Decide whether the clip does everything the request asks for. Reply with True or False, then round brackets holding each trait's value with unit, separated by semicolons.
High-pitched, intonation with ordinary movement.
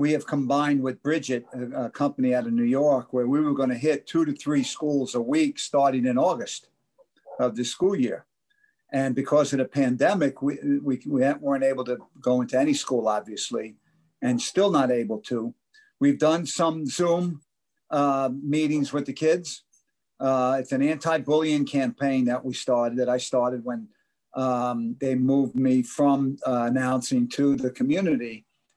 False (135 Hz; 3.3 semitones)